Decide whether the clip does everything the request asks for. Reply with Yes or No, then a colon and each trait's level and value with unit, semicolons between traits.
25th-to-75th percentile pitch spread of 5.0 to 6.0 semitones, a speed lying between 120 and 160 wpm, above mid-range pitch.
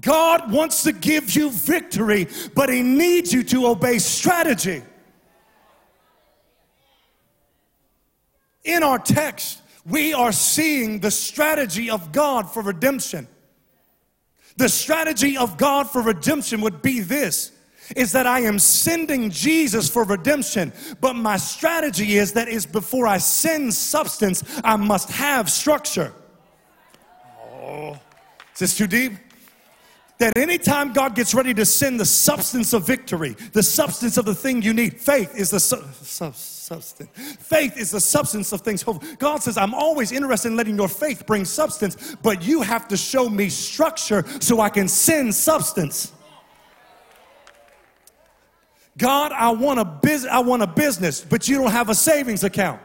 Yes: wide, 5.5 semitones; average, 150 wpm; high, 240 Hz